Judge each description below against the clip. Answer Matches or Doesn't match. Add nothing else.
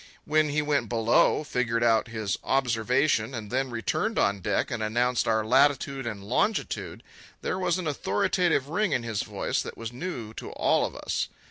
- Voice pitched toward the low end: Matches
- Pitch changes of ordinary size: Matches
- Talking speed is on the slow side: Doesn't match